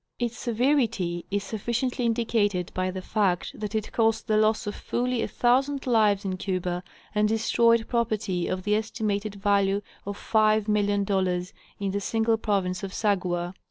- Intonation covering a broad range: No, average, 2.7 semitones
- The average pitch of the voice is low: No, high, 210 Hz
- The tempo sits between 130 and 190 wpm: Yes, average, 155 wpm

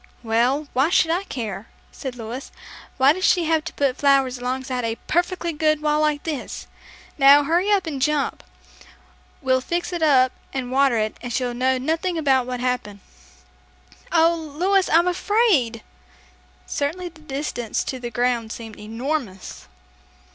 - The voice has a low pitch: No, very high, 275 Hz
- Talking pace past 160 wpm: No, average, 155 wpm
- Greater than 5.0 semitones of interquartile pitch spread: No, average, 4.5 semitones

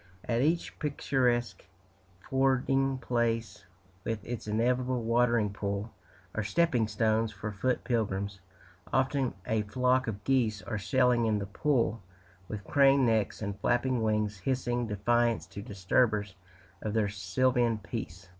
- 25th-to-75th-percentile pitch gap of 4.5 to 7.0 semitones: No, average, 3.4 semitones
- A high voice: No, low, 115 Hz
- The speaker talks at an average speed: No, slow, 130 wpm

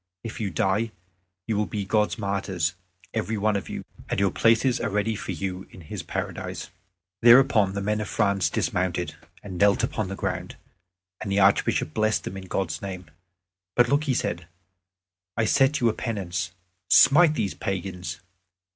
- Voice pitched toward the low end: Yes, low, 100 Hz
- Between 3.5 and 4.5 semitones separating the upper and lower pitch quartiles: No, average, 3.0 semitones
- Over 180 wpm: No, average, 170 wpm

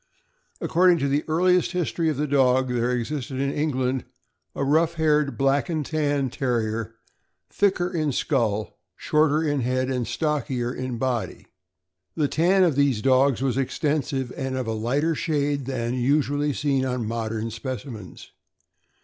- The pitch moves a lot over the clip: No, average, 3.4 semitones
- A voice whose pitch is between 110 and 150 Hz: Yes, low, 135 Hz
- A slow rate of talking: No, average, 155 wpm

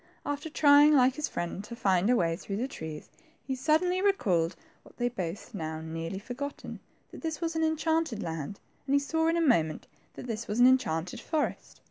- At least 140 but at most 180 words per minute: No, average, 200 wpm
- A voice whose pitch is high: Yes, high, 245 Hz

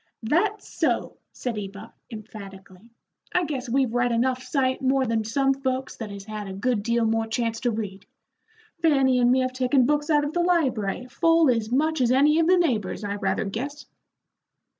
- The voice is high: Yes, very high, 250 Hz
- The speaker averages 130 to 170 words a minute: No, average, 185 wpm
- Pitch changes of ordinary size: Yes, average, 4.0 semitones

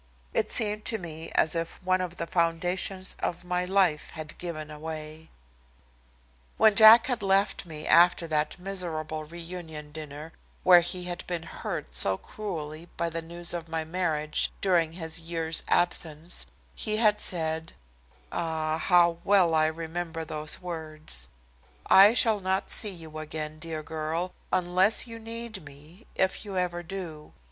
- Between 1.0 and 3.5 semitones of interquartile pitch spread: Yes, average, 2.8 semitones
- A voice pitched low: No, medium, 170 Hz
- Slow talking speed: No, average, 150 wpm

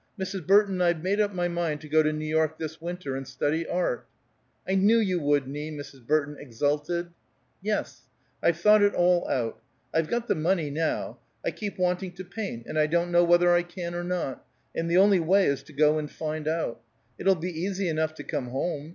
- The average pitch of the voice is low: No, medium, 170 Hz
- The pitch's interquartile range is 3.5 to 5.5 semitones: No, average, 3.1 semitones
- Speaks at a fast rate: Yes, fast, 210 wpm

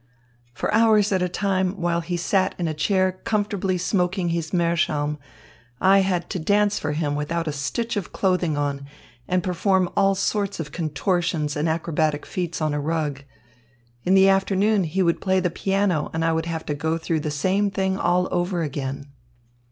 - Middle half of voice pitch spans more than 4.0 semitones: No, average, 3.5 semitones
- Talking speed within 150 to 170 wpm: No, average, 185 wpm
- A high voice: No, medium, 175 Hz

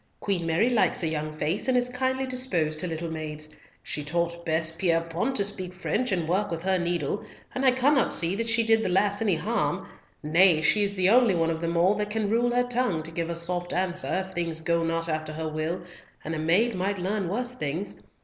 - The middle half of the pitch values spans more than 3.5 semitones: Yes, average, 4.5 semitones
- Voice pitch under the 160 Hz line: No, medium, 180 Hz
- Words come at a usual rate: No, fast, 225 wpm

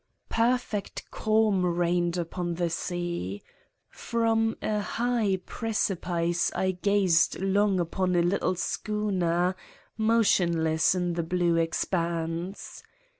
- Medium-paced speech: No, slow, 100 wpm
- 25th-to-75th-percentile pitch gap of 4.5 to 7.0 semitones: No, average, 3.5 semitones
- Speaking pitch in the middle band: Yes, medium, 180 Hz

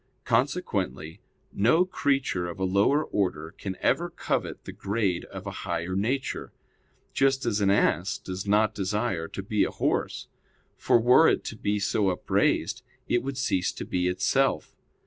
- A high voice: No, low, 100 Hz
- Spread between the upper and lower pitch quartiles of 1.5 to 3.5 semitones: No, average, 4.8 semitones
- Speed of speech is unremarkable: Yes, average, 160 wpm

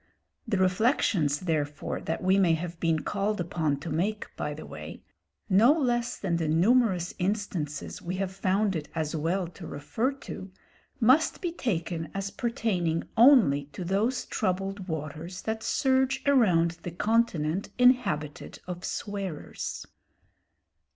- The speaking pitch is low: No, medium, 185 Hz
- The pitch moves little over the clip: No, average, 5.2 semitones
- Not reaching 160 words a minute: Yes, slow, 135 wpm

